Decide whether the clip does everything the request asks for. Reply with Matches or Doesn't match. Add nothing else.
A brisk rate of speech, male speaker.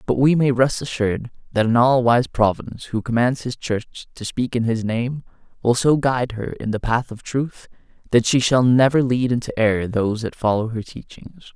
Matches